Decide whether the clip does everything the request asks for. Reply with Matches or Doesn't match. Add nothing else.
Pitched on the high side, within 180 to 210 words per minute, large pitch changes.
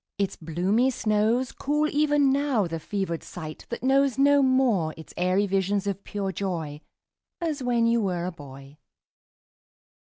Doesn't match